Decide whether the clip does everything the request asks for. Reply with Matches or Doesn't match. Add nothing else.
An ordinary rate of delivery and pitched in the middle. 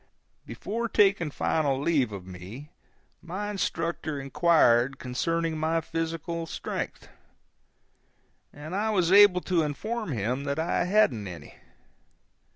Doesn't match